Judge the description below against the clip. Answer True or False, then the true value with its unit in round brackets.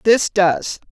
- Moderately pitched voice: False (200 Hz)